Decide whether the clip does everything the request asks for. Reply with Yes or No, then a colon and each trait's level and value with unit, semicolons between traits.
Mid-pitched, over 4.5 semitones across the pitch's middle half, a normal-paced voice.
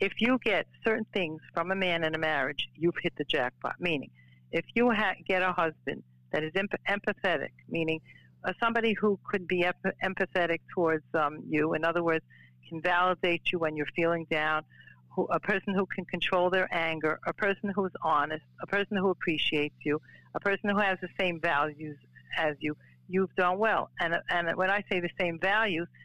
No: medium, 175 Hz; average, 3.8 semitones; average, 195 wpm